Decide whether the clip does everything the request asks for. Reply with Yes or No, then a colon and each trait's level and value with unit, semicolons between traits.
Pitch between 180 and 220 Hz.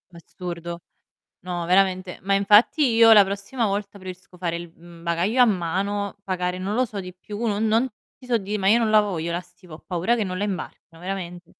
Yes: high, 190 Hz